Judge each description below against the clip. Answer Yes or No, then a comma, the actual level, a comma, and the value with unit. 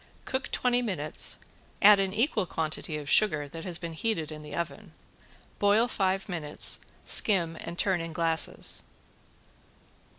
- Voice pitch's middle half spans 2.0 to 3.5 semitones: No, average, 4.3 semitones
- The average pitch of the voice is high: No, medium, 175 Hz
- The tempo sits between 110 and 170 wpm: Yes, average, 140 wpm